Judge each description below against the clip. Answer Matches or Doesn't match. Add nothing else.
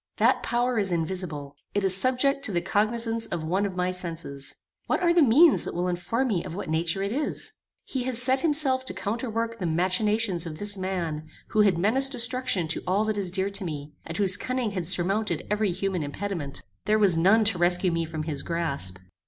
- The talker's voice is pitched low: Doesn't match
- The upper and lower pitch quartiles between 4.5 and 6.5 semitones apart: Matches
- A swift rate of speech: Matches